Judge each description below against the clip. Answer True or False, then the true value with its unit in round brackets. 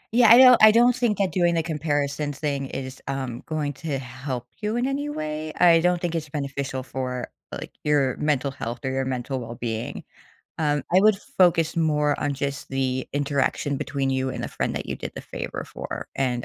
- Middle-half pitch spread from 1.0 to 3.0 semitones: False (4.0 semitones)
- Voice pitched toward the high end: False (145 Hz)